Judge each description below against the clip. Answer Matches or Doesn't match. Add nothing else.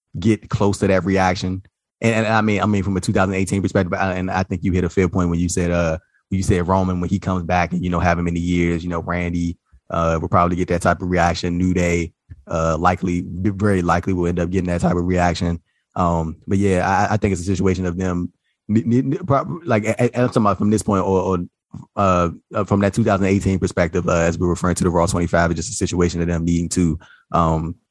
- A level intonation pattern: Matches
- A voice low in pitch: Matches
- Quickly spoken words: Matches